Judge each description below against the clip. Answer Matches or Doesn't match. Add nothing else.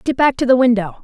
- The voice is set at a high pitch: Matches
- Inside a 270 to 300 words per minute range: Matches